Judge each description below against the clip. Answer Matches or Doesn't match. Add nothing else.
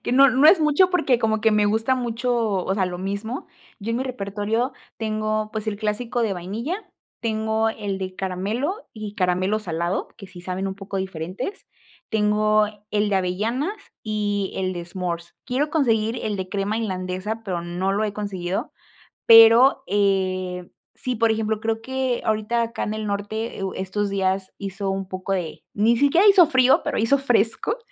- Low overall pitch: Doesn't match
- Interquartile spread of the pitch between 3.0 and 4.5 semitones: Matches